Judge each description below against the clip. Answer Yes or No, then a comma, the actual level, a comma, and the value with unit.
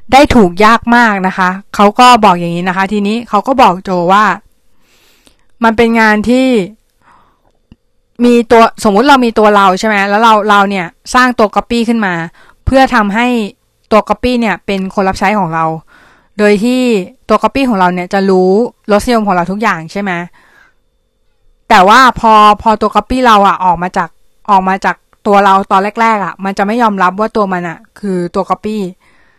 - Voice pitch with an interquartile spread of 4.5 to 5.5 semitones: No, average, 3.2 semitones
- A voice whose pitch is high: Yes, high, 210 Hz